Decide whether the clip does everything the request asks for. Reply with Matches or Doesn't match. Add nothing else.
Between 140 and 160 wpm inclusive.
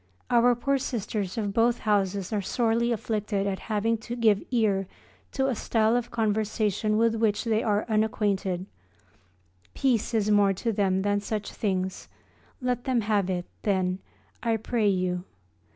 Matches